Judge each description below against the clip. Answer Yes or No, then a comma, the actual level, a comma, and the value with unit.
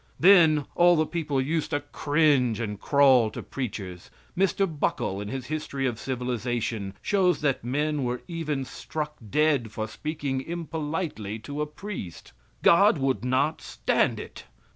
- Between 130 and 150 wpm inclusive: Yes, average, 145 wpm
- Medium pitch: Yes, medium, 145 Hz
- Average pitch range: Yes, average, 4.3 semitones